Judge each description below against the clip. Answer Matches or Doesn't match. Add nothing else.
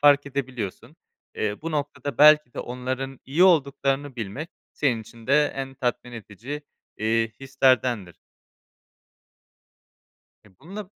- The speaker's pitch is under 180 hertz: Matches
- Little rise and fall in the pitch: Doesn't match